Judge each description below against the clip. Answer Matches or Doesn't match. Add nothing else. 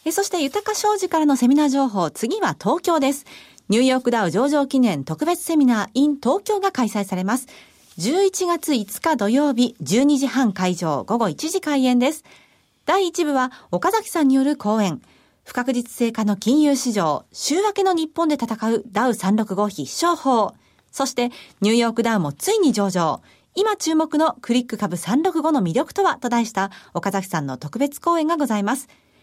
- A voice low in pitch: Doesn't match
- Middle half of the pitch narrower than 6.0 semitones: Doesn't match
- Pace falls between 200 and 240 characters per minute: Doesn't match